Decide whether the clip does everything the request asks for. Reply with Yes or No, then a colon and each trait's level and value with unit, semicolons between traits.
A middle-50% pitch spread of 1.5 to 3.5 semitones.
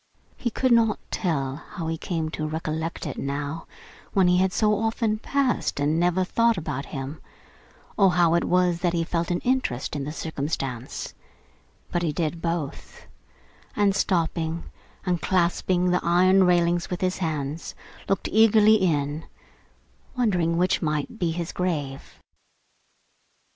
Yes: average, 3.1 semitones